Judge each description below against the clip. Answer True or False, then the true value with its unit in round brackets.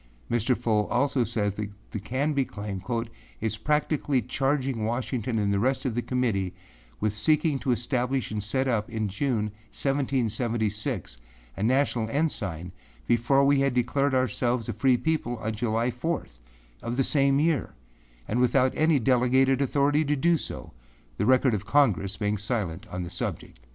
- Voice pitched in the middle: False (120 Hz)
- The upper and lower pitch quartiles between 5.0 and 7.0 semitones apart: False (4.1 semitones)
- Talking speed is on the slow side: False (160 wpm)